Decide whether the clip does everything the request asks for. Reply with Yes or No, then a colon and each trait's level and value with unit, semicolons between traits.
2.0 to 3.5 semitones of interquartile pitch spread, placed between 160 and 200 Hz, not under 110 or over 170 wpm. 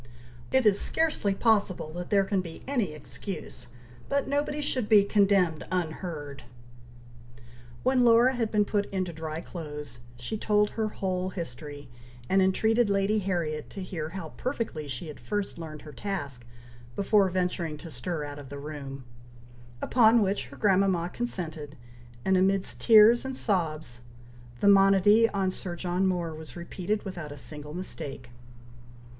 No: average, 5.1 semitones; medium, 185 Hz; average, 150 wpm